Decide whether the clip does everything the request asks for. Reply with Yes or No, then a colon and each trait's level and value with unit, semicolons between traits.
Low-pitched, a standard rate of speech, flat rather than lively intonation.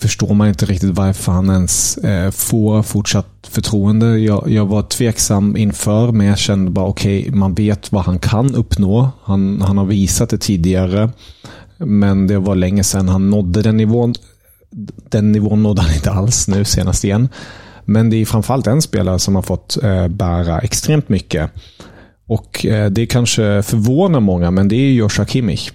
Yes: low, 105 Hz; average, 165 wpm; narrow, 2.3 semitones